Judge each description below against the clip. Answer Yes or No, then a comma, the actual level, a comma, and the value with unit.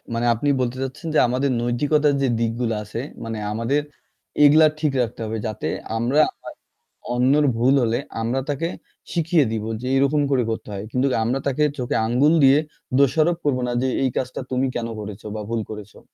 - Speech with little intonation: No, average, 3.7 semitones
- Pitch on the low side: Yes, low, 125 Hz